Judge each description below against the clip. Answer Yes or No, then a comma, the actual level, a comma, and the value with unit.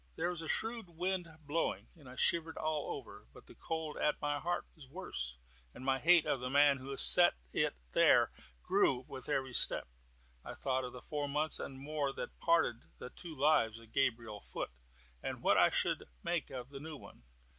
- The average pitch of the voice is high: No, medium, 145 Hz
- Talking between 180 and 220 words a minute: Yes, average, 200 wpm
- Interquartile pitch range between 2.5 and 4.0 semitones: Yes, average, 3.7 semitones